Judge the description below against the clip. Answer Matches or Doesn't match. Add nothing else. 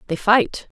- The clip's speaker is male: Doesn't match